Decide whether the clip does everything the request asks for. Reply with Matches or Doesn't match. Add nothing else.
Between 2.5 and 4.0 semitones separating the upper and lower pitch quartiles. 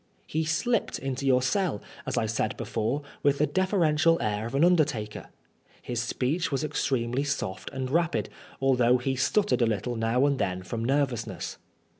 Doesn't match